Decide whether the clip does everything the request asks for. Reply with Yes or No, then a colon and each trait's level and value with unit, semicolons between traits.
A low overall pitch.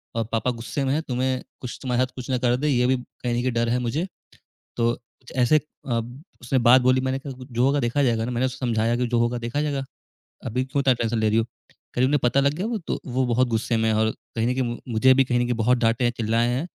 Yes: low, 125 Hz